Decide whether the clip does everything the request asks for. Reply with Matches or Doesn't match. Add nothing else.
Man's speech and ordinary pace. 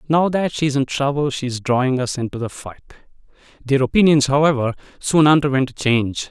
Matches